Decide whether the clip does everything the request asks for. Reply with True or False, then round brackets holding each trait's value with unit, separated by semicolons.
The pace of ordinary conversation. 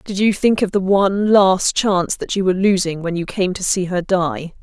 False (245 wpm)